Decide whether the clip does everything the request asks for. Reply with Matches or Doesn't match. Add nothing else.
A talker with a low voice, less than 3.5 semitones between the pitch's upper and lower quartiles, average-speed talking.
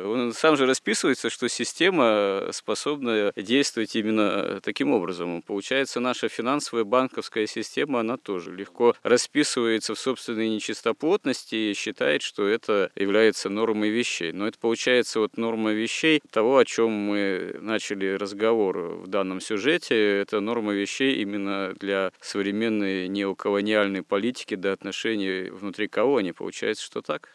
Matches